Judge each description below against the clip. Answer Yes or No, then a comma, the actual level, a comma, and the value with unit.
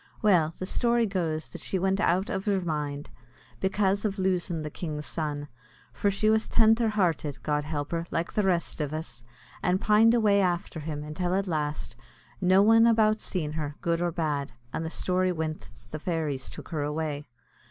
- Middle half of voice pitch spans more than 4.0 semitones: Yes, average, 4.4 semitones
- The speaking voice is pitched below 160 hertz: No, medium, 175 Hz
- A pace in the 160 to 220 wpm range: Yes, average, 190 wpm